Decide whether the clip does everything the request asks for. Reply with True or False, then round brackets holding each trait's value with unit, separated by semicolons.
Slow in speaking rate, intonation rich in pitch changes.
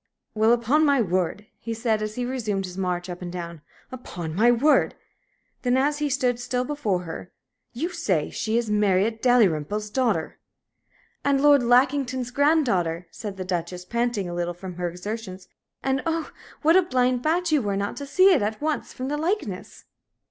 False (180 wpm; 6.5 semitones)